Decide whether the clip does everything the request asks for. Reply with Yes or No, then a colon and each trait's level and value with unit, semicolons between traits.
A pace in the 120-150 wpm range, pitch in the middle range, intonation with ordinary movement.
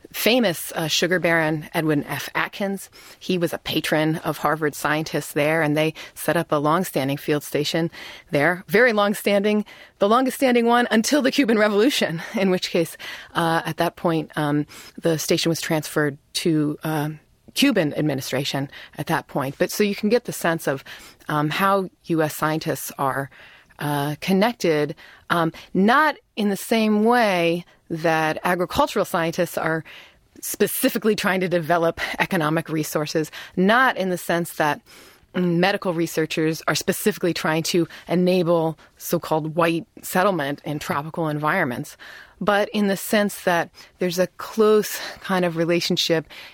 Yes: average, 145 wpm; medium, 170 Hz; average, 3.9 semitones